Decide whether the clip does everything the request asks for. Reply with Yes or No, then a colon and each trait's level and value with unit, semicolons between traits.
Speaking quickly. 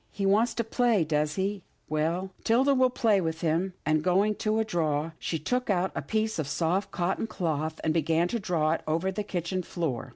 Yes: fast, 215 wpm